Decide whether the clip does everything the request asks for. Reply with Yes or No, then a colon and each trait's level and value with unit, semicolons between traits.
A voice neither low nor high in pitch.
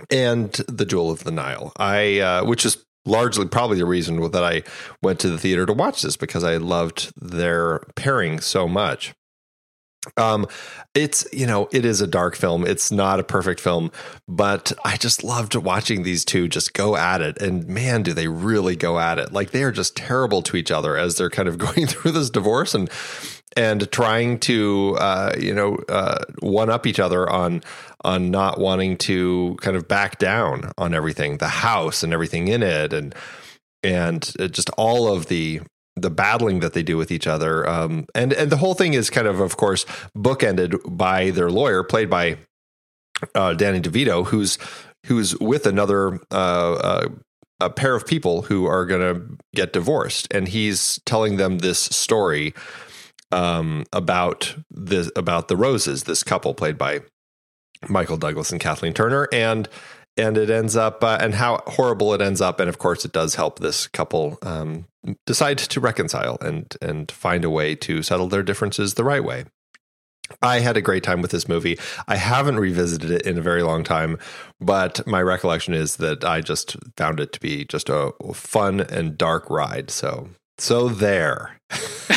No: very low, 95 Hz